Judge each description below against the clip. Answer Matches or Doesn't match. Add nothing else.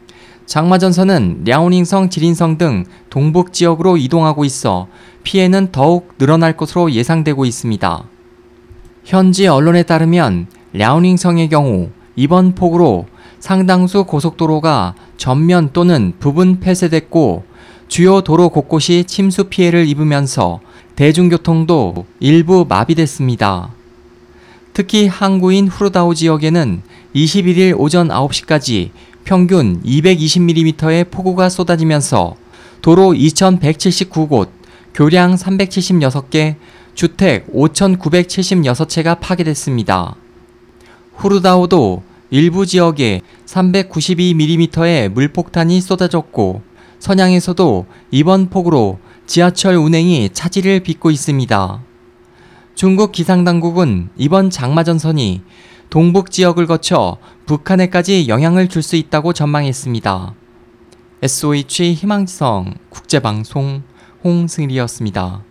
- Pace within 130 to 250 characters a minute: Matches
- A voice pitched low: Doesn't match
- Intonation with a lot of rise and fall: Matches